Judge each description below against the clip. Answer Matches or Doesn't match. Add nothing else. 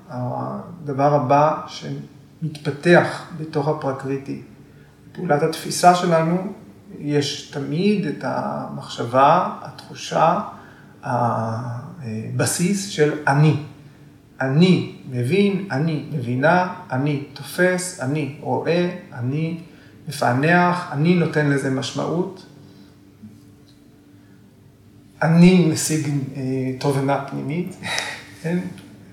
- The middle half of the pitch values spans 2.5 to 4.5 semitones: Matches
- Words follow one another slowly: Matches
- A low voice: Doesn't match